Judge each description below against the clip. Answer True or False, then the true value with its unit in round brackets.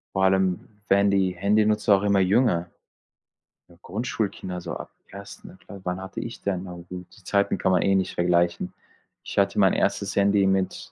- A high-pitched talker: False (95 Hz)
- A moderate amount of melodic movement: False (1.8 semitones)